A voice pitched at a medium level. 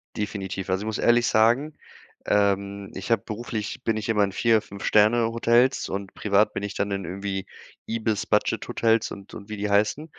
No: low, 105 Hz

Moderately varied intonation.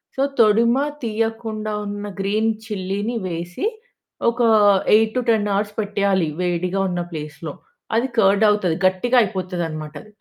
Yes: average, 3.5 semitones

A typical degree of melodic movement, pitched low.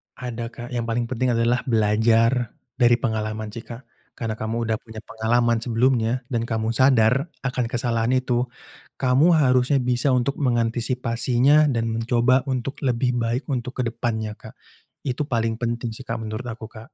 No: narrow, 1.9 semitones; low, 120 Hz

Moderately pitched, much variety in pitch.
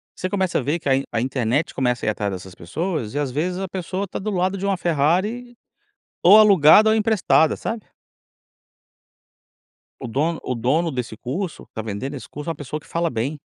Yes: medium, 155 Hz; wide, 6.6 semitones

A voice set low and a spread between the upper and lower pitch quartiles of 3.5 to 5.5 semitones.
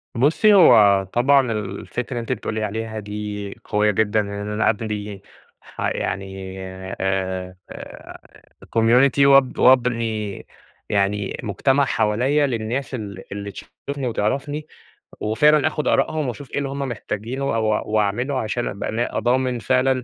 Yes: low, 115 Hz; average, 4.1 semitones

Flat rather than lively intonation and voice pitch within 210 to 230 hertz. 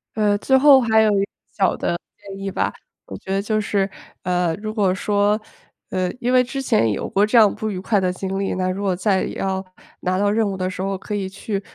No: narrow, 2.2 semitones; high, 200 Hz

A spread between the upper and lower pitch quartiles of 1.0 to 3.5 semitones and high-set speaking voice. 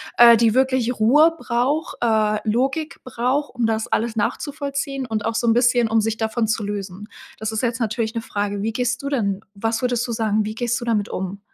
Yes: narrow, 2.5 semitones; high, 230 Hz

